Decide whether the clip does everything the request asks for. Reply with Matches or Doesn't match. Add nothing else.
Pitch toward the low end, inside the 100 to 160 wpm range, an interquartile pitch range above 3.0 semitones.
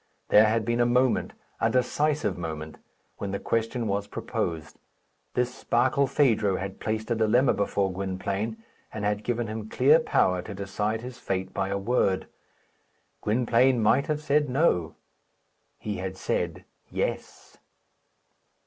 Matches